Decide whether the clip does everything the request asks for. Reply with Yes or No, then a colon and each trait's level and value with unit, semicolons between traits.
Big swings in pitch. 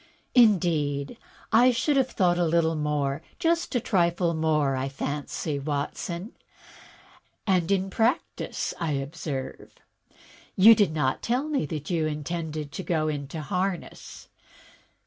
No: average, 4.8 semitones